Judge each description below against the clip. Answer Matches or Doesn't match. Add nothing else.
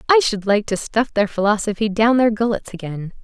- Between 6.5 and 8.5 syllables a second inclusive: Doesn't match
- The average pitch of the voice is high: Matches